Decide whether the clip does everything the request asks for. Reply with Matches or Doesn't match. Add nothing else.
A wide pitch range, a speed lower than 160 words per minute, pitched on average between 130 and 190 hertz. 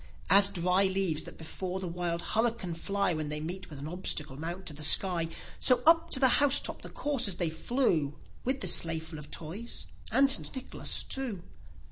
Doesn't match